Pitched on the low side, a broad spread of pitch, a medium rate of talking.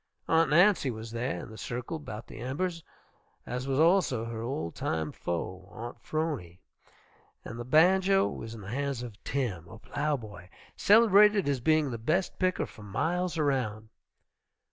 Yes: low, 130 Hz; wide, 6.7 semitones; average, 165 wpm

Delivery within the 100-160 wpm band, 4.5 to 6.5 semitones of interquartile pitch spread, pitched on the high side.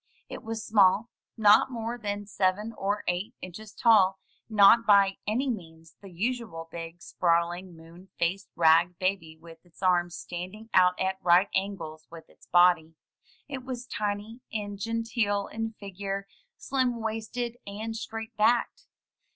No: average, 150 wpm; average, 4.0 semitones; high, 200 Hz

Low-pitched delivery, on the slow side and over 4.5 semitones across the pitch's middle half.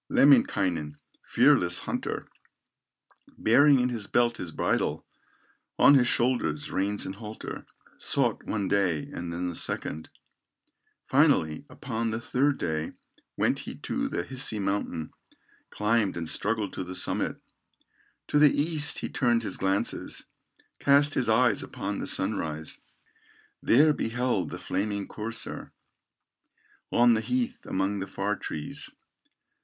Yes: low, 105 Hz; slow, 130 wpm; average, 4.9 semitones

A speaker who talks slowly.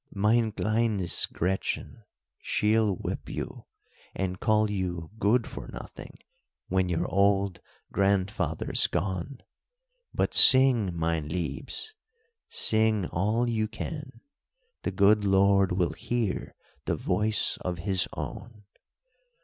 Yes: slow, 110 wpm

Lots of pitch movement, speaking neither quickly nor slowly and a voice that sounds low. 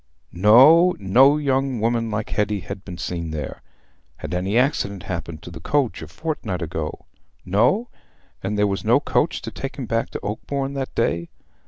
Yes: wide, 7.2 semitones; average, 175 wpm; low, 105 Hz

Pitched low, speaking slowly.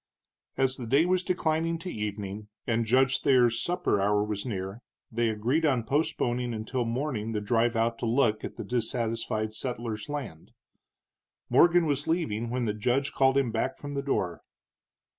No: low, 120 Hz; average, 165 wpm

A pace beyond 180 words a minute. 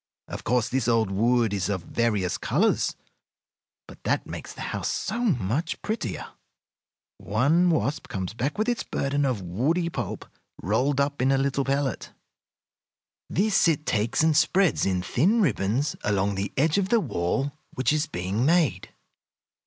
No: average, 160 wpm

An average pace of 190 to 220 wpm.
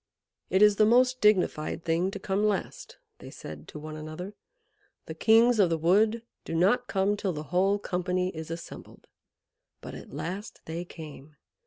No: average, 170 wpm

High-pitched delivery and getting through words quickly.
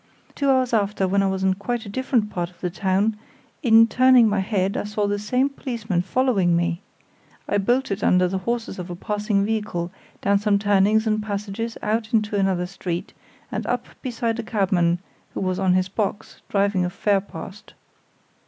No: high, 205 Hz; average, 185 wpm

